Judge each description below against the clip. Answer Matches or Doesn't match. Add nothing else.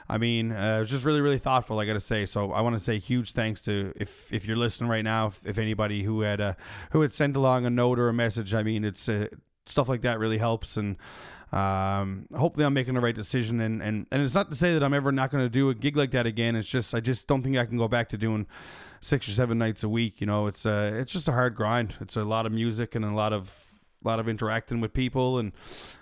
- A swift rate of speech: Matches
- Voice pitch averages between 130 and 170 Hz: Doesn't match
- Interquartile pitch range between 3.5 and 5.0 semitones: Doesn't match